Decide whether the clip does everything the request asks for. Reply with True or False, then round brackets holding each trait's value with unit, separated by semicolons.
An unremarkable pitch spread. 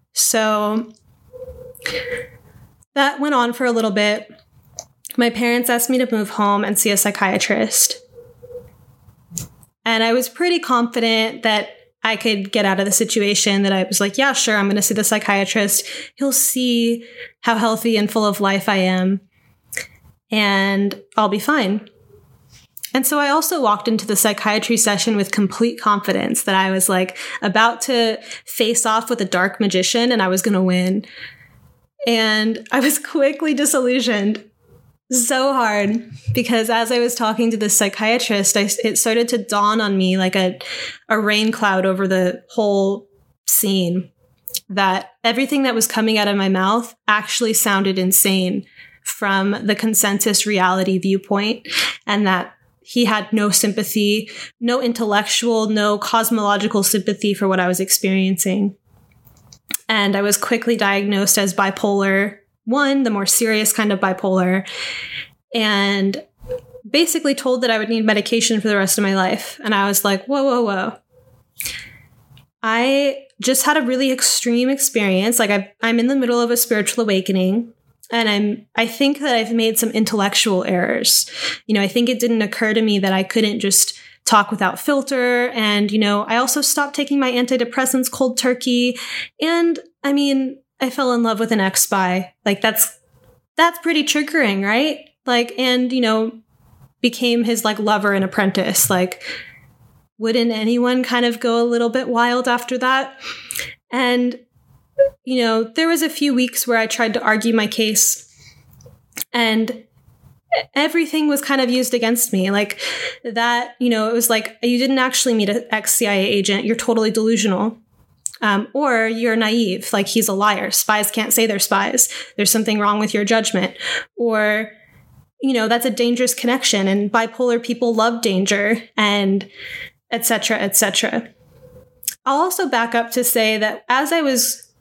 True (3.4 semitones)